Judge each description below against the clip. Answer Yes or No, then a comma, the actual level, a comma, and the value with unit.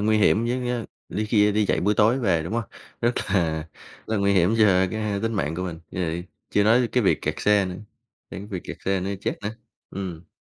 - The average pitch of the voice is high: No, low, 100 Hz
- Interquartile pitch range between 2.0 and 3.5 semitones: Yes, average, 3.0 semitones